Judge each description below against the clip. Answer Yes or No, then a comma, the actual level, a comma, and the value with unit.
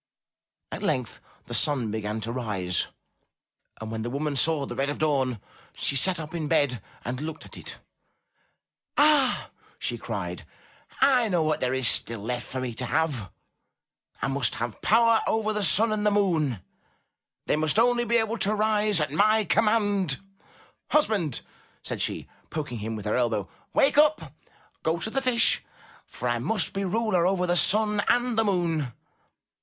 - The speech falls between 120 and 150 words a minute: No, average, 170 wpm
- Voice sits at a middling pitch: Yes, medium, 160 Hz